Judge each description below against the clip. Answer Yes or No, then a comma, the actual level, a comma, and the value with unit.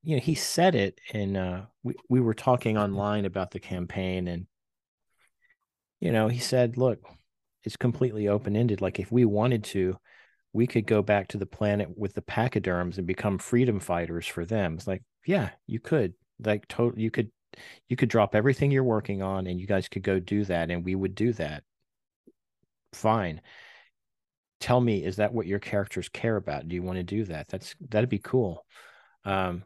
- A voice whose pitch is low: Yes, low, 105 Hz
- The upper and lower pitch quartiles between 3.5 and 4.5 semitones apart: Yes, average, 3.8 semitones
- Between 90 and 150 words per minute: No, average, 190 wpm